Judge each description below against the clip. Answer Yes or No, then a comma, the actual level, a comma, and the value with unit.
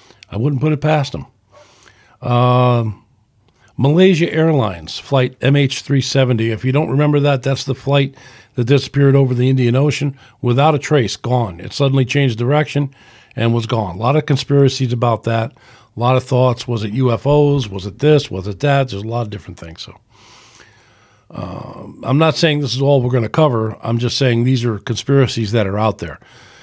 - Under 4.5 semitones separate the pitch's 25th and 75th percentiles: Yes, average, 3.6 semitones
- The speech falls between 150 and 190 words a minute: Yes, average, 185 wpm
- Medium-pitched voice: No, low, 125 Hz